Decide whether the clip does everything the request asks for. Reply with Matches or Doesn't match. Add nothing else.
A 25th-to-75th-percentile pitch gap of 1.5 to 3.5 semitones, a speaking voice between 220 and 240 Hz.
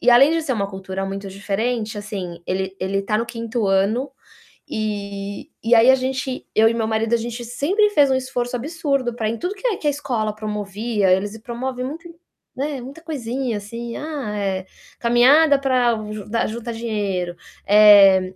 Doesn't match